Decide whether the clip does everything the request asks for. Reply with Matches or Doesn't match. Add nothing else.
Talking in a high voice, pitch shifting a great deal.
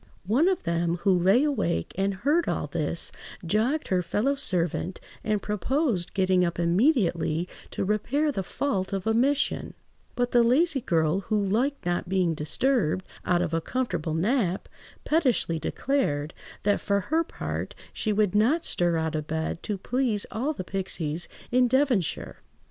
Matches